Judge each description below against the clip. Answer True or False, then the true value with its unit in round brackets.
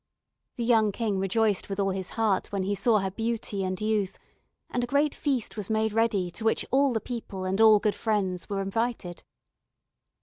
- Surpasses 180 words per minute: True (195 wpm)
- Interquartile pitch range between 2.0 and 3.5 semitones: True (2.8 semitones)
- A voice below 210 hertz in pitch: False (215 Hz)